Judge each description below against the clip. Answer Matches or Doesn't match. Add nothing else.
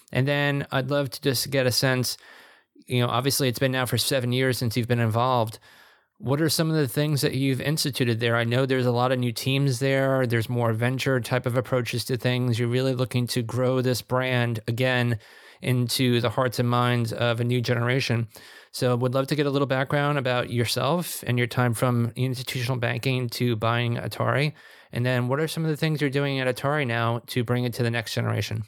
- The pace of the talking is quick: Matches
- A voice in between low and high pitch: Doesn't match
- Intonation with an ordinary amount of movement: Doesn't match